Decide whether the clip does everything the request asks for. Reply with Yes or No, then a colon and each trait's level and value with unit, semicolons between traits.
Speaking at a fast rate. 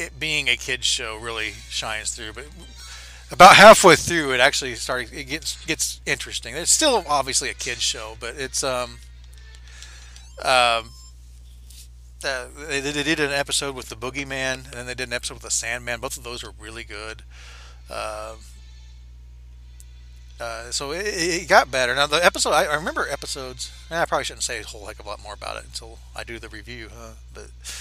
No: average, 190 wpm